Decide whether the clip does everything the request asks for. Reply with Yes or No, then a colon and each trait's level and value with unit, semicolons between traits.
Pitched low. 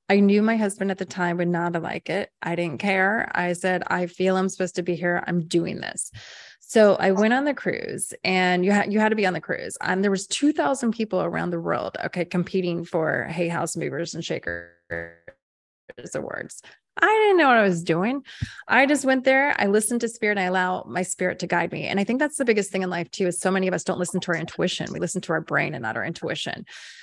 No: medium, 185 Hz